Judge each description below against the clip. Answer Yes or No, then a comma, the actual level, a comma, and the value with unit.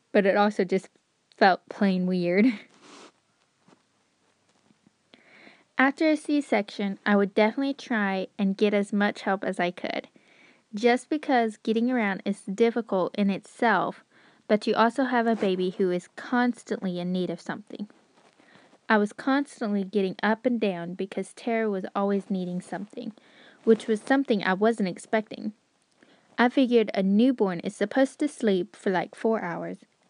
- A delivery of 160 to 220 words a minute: No, average, 150 wpm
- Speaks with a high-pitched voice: Yes, high, 215 Hz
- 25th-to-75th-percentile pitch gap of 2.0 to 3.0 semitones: No, average, 3.5 semitones